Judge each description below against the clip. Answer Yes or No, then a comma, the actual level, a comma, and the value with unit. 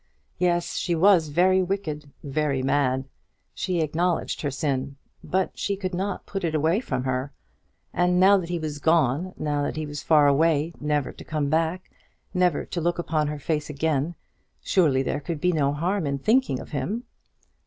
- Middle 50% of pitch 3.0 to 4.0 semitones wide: Yes, average, 3.7 semitones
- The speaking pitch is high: No, medium, 160 Hz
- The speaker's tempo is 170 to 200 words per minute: Yes, average, 180 wpm